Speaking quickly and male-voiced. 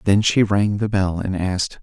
Yes: fast, 230 wpm; male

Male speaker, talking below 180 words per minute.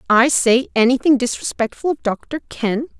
No: female; average, 140 wpm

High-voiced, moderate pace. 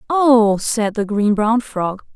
Yes: high, 220 Hz; average, 165 wpm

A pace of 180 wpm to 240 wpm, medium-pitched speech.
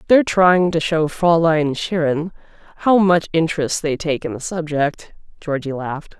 No: average, 155 wpm; medium, 160 Hz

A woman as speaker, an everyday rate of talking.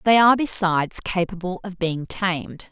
Yes: female; average, 155 wpm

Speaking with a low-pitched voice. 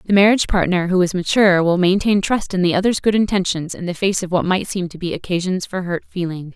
No: medium, 185 Hz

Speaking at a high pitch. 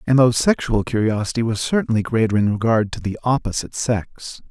No: low, 115 Hz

